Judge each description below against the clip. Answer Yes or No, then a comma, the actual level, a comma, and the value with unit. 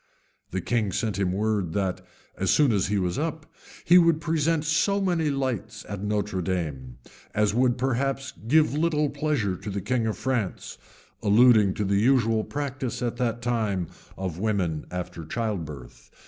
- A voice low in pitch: Yes, low, 110 Hz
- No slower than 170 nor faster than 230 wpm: No, average, 160 wpm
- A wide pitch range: Yes, wide, 6.1 semitones